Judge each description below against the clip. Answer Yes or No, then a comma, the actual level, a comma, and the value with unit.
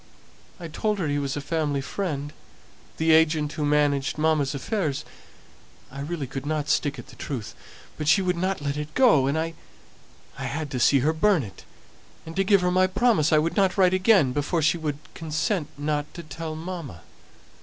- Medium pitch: Yes, medium, 155 Hz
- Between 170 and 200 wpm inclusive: Yes, average, 185 wpm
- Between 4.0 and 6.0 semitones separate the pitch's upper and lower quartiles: No, average, 3.5 semitones